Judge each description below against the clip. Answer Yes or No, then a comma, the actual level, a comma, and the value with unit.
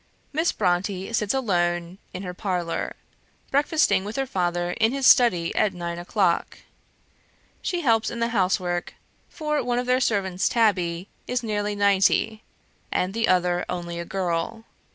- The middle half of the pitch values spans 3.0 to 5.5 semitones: Yes, average, 4.7 semitones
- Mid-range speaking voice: No, high, 195 Hz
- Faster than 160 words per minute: No, average, 150 wpm